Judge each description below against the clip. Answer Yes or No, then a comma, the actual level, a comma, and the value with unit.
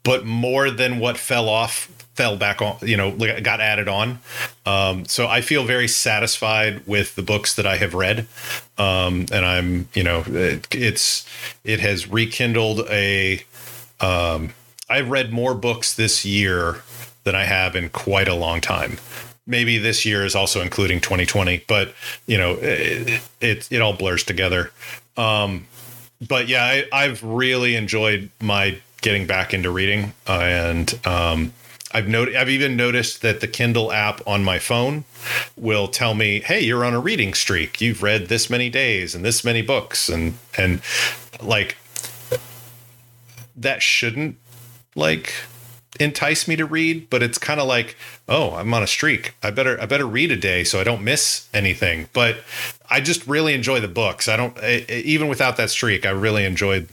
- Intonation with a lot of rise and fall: No, average, 3.8 semitones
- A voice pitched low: Yes, low, 115 Hz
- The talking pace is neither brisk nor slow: Yes, average, 175 wpm